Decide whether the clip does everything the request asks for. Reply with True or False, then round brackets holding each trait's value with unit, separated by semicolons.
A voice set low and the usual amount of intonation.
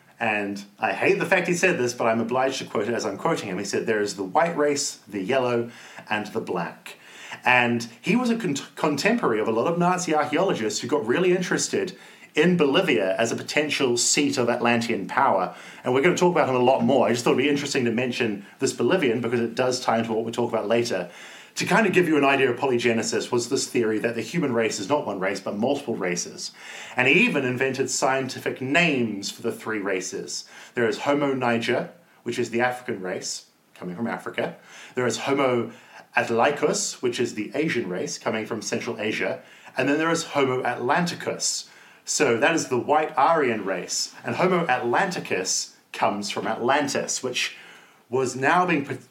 True (125 Hz; 3.8 semitones)